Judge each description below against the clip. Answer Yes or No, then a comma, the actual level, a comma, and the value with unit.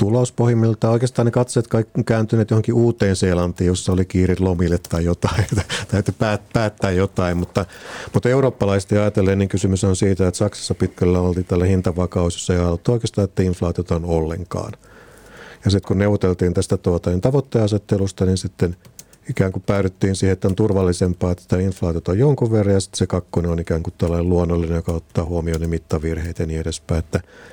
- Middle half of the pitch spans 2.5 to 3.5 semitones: Yes, average, 2.9 semitones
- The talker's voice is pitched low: Yes, very low, 95 Hz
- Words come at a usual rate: No, fast, 175 wpm